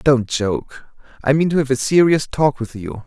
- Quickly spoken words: Yes, fast, 215 wpm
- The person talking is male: Yes, male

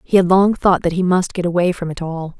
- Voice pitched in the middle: Yes, medium, 175 Hz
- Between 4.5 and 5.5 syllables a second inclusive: No, 5.8 syllables/s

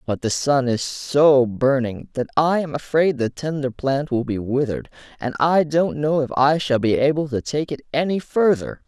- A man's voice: Yes, male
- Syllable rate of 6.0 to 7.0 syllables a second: No, 4.7 syllables/s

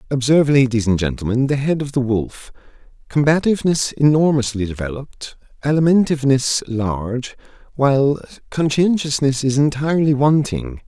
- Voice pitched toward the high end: No, low, 135 Hz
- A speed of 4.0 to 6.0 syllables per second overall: Yes, 5.3 syllables/s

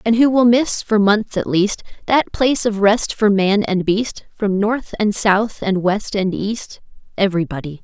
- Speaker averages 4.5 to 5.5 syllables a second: No, 4.3 syllables/s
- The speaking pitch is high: Yes, high, 205 Hz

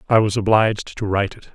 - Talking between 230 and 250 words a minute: Yes, fast, 235 wpm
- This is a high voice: No, low, 105 Hz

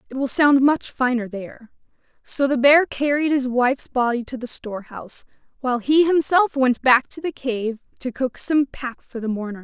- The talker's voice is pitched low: No, very high, 260 Hz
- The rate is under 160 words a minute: No, average, 195 wpm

